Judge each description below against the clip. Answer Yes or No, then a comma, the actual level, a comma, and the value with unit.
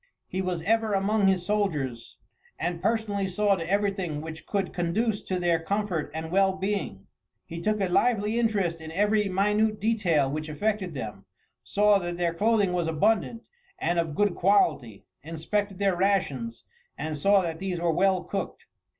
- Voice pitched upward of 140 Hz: Yes, high, 190 Hz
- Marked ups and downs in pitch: No, average, 3.8 semitones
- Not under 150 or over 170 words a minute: Yes, average, 165 wpm